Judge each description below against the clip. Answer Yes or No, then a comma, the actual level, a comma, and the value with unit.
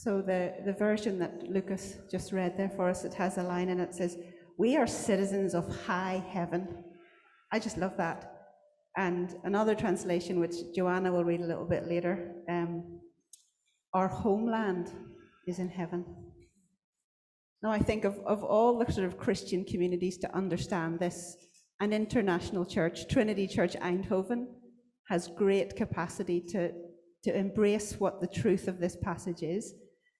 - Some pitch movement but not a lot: No, narrow, 2.3 semitones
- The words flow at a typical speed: Yes, average, 155 wpm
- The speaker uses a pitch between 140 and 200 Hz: Yes, medium, 185 Hz